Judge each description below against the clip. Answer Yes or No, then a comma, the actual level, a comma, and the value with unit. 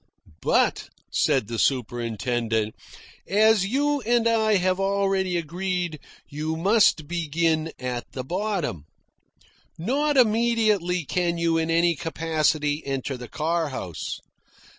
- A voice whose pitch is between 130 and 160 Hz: No, medium, 170 Hz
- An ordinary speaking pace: No, slow, 115 wpm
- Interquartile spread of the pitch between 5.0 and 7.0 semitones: Yes, wide, 5.4 semitones